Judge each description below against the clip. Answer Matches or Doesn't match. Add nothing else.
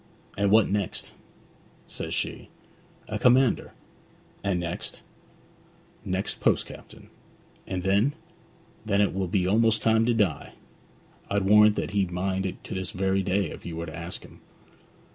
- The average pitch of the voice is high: Doesn't match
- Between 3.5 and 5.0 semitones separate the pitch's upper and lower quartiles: Doesn't match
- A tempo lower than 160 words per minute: Matches